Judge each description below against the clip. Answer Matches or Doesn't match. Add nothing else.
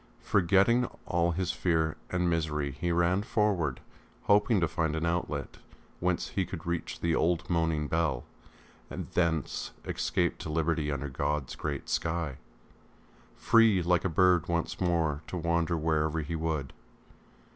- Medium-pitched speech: Doesn't match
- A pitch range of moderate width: Doesn't match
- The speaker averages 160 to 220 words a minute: Doesn't match